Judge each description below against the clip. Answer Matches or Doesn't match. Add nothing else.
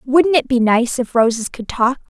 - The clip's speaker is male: Doesn't match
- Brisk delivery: Matches